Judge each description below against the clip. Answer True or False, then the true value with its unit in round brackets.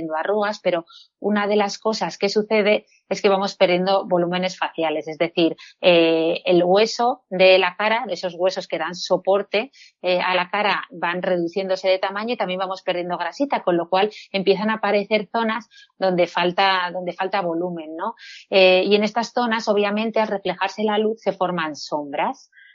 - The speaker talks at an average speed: True (175 wpm)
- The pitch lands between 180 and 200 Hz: True (190 Hz)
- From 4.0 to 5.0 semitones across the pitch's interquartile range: False (2.9 semitones)